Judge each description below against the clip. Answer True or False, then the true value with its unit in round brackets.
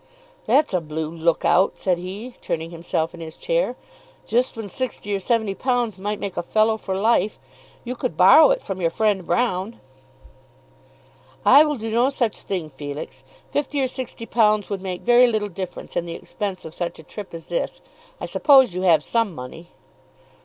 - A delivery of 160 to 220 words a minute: True (180 wpm)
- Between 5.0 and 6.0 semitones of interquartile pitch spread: True (5.6 semitones)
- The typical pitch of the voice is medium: False (200 Hz)